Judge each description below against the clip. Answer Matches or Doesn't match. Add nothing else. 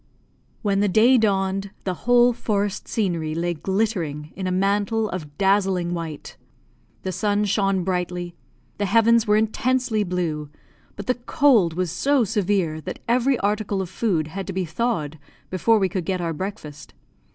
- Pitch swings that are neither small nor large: Matches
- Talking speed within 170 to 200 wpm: Doesn't match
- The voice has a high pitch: Matches